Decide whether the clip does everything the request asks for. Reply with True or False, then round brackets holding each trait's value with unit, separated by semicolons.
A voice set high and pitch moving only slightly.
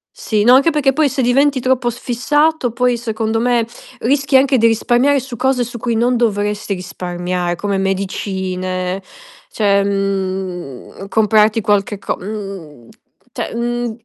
False (220 Hz; 4.2 semitones)